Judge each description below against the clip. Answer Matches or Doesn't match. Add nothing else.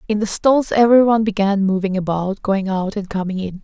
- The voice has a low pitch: Doesn't match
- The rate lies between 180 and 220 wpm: Matches